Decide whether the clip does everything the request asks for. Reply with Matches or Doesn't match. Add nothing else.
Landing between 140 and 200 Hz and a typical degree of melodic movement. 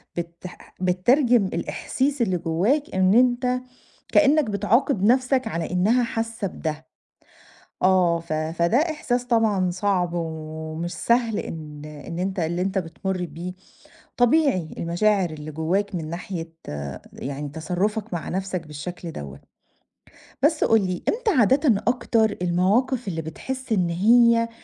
Doesn't match